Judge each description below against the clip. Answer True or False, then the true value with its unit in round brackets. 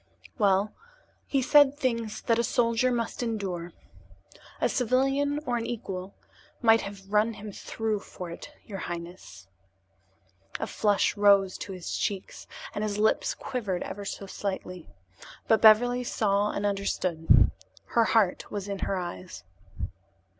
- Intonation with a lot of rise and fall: False (3.2 semitones)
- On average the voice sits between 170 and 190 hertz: False (210 Hz)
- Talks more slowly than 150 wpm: True (140 wpm)